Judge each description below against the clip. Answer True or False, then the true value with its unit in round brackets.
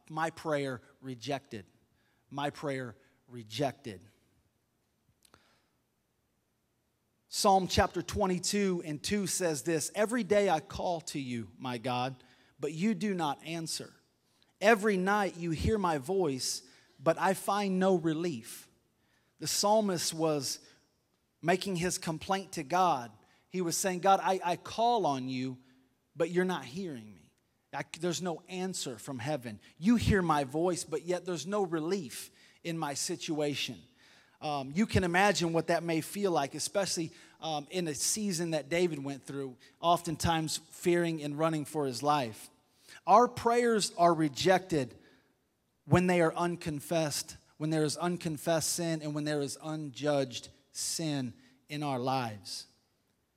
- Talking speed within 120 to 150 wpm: True (140 wpm)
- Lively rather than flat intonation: False (4.9 semitones)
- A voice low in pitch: False (155 Hz)